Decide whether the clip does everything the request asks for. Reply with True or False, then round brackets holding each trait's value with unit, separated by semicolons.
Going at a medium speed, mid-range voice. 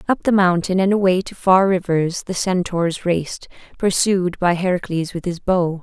True (175 wpm; 180 Hz)